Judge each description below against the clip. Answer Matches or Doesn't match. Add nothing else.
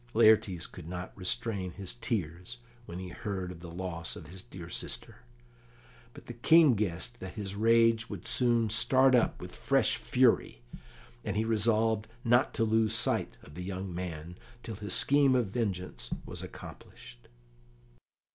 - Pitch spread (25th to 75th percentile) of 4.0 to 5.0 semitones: Matches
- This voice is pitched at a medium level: Doesn't match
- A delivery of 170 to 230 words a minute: Doesn't match